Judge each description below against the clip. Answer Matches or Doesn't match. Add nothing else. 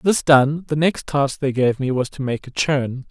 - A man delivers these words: Matches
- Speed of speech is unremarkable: Doesn't match